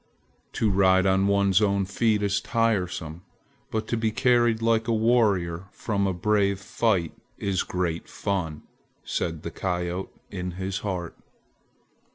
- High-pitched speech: No, low, 100 Hz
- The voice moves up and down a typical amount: Yes, average, 3.2 semitones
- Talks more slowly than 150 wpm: Yes, average, 140 wpm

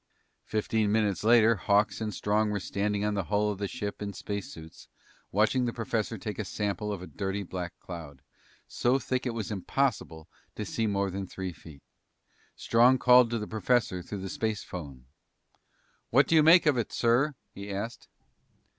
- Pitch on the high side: No, low, 105 Hz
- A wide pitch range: No, average, 3.1 semitones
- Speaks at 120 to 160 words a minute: No, average, 180 wpm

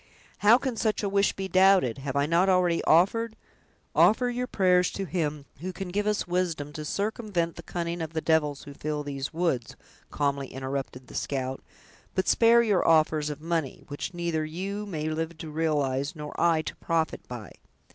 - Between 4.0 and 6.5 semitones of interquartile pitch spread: Yes, average, 4.4 semitones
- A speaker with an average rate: Yes, average, 185 wpm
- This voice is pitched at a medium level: Yes, medium, 165 Hz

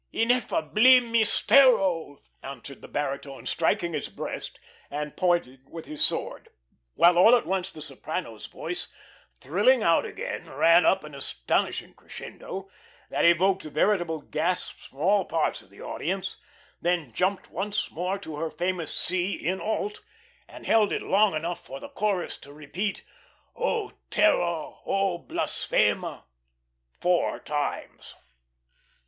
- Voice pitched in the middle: Yes, medium, 175 Hz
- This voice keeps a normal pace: No, slow, 130 wpm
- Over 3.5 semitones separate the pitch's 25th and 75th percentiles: Yes, average, 4.5 semitones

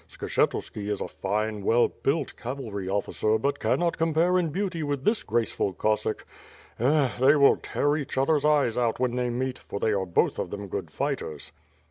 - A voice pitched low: Yes, low, 125 Hz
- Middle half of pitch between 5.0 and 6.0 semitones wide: Yes, wide, 5.5 semitones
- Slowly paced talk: No, average, 180 wpm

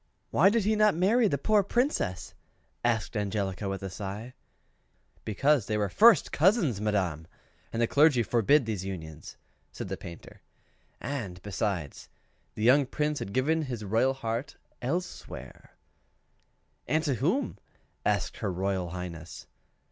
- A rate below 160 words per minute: Yes, average, 140 wpm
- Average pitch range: No, wide, 7.6 semitones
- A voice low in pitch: Yes, low, 115 Hz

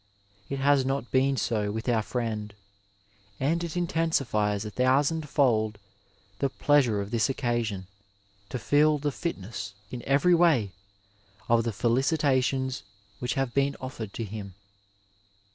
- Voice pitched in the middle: No, low, 130 Hz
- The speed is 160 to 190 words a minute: No, slow, 135 wpm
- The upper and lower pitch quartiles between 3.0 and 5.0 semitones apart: Yes, average, 4.4 semitones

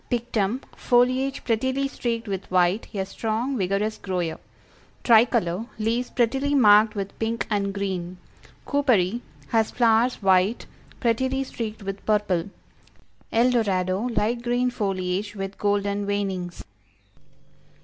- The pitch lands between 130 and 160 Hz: No, high, 215 Hz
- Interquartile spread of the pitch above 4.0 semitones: No, average, 3.7 semitones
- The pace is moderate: No, slow, 115 wpm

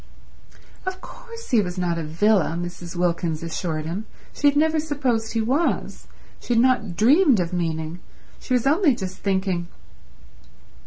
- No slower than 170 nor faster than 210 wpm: No, average, 155 wpm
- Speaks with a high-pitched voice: Yes, high, 200 Hz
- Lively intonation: Yes, wide, 7.7 semitones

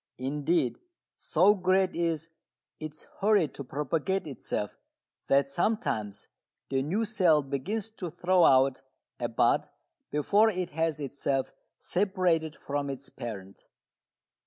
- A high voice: No, medium, 155 Hz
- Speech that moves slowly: Yes, slow, 115 wpm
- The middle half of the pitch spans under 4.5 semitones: No, average, 5.2 semitones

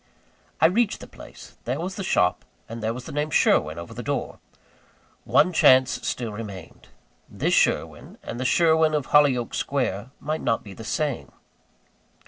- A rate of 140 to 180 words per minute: Yes, average, 160 wpm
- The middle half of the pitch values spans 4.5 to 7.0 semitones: Yes, wide, 5.6 semitones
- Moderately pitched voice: No, low, 130 Hz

